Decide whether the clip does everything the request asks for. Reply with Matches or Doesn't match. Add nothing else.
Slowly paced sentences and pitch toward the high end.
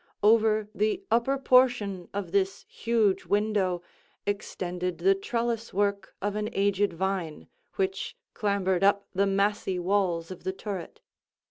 Matches